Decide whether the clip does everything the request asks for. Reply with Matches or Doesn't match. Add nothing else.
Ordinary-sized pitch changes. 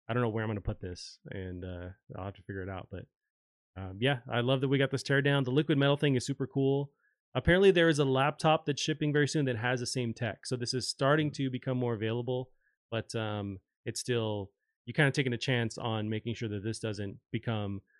Matches